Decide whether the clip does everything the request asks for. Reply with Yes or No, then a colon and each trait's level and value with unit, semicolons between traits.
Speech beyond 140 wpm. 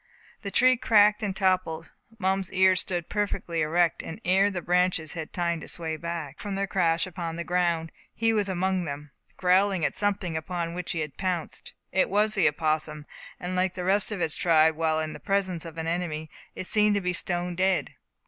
Yes: fast, 205 wpm